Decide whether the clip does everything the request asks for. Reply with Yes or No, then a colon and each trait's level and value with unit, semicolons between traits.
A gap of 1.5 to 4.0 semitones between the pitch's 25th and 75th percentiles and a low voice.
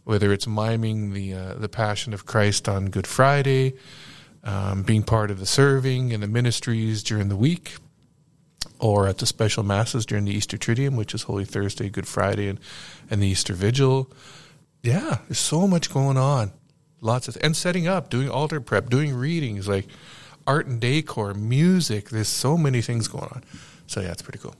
No: average, 5.1 semitones; low, 120 Hz